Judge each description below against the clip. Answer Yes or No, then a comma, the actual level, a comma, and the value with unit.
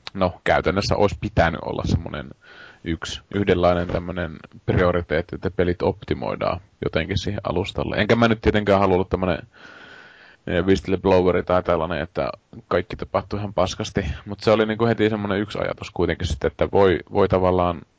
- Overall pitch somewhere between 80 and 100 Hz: Yes, very low, 95 Hz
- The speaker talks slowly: No, average, 145 wpm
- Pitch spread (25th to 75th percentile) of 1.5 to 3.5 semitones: Yes, average, 2.8 semitones